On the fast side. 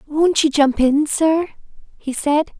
No: average, 160 wpm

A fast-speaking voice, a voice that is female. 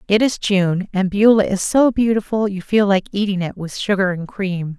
Yes: fast, 215 wpm; female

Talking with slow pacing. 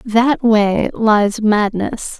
Yes: slow, 110 wpm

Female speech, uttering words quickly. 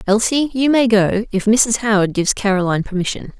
No: female; average, 175 wpm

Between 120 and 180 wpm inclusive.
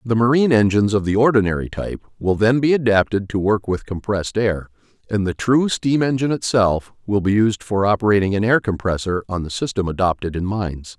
No: average, 195 wpm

